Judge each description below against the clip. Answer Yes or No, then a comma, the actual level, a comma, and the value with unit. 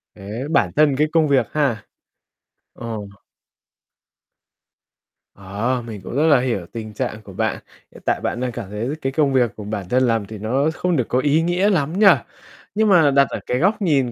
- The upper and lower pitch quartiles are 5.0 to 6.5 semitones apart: Yes, wide, 5.6 semitones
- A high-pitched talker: No, low, 130 Hz